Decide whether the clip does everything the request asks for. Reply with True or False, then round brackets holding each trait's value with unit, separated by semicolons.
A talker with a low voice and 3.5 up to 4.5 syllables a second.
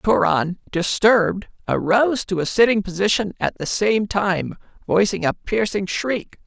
False (195 Hz; 4.4 syllables/s)